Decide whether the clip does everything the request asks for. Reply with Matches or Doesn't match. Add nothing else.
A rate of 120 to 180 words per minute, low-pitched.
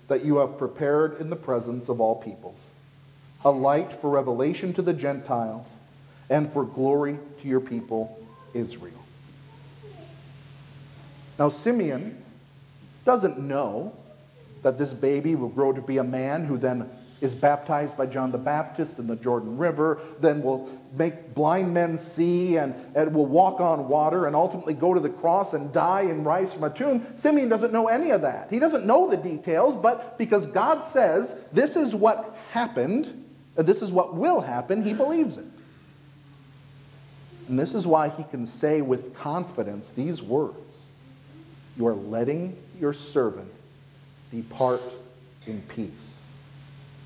Doesn't match